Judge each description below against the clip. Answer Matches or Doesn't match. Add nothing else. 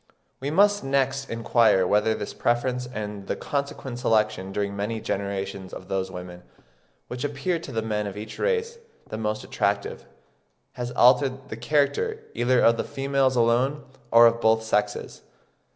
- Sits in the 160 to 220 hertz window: Doesn't match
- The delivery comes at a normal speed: Matches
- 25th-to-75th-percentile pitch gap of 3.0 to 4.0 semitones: Doesn't match